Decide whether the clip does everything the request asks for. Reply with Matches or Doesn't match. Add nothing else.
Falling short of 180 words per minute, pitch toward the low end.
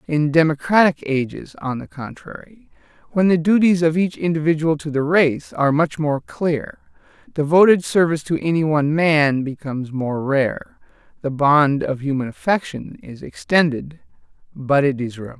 Doesn't match